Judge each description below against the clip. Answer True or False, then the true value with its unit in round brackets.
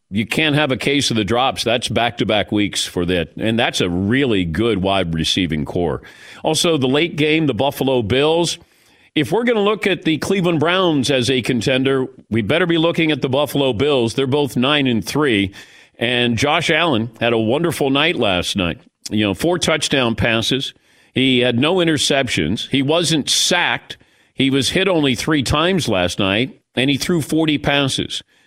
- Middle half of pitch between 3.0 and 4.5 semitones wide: False (5.1 semitones)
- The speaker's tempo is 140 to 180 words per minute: False (190 wpm)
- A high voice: False (135 Hz)